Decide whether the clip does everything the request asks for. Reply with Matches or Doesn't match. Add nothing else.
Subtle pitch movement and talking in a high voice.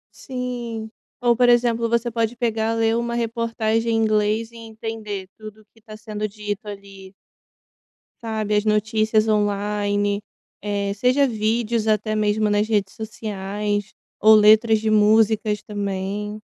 Matches